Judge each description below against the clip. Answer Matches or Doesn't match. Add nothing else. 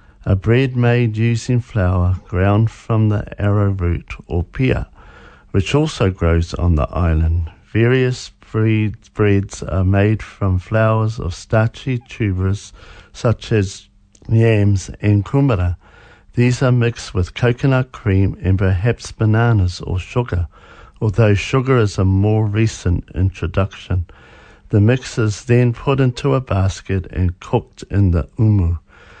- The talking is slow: Matches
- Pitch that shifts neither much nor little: Matches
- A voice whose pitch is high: Doesn't match